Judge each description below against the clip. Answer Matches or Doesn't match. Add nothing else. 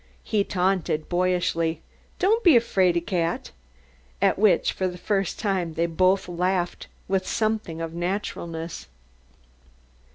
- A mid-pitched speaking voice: Matches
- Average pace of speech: Doesn't match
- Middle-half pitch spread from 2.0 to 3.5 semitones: Matches